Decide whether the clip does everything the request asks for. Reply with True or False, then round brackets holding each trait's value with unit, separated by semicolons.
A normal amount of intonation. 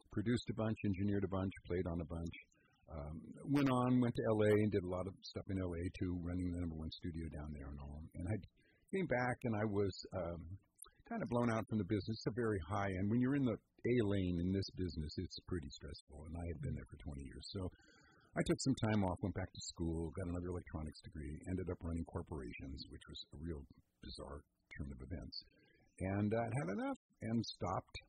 True (4.5 semitones)